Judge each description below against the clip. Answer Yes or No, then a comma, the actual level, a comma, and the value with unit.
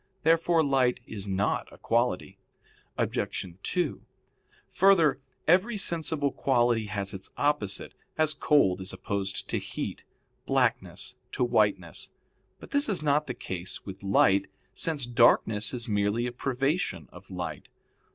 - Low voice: Yes, low, 120 Hz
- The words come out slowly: Yes, slow, 130 wpm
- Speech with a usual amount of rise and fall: No, wide, 7.2 semitones